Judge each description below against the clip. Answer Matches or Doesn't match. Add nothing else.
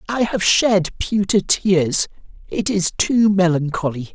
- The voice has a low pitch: Doesn't match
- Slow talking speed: Matches